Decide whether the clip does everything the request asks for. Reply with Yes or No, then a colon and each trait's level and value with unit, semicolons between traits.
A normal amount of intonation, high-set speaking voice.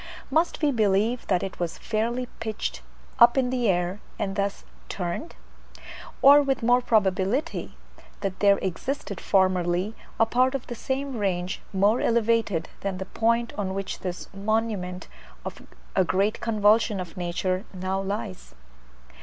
Yes: average, 3.9 semitones; high, 205 Hz